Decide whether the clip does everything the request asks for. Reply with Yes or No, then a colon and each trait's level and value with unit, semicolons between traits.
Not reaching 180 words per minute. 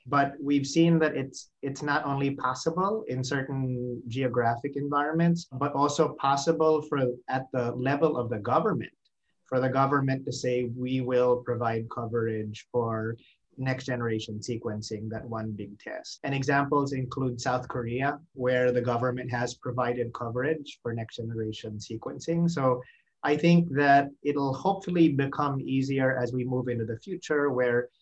Yes: average, 150 wpm